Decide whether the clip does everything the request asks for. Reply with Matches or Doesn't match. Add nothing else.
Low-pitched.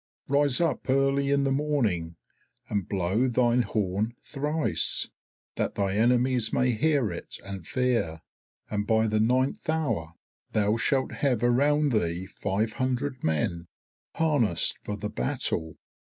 Matches